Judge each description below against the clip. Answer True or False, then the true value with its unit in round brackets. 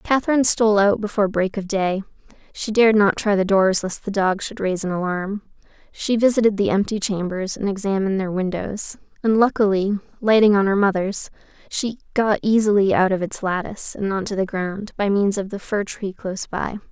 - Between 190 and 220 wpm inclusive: True (195 wpm)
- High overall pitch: True (200 Hz)